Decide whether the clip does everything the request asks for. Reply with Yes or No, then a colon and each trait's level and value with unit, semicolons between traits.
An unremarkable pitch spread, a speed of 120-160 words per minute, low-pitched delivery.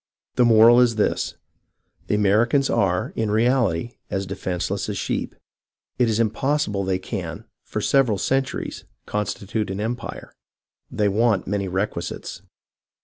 Yes: average, 3.4 semitones; average, 140 wpm; low, 105 Hz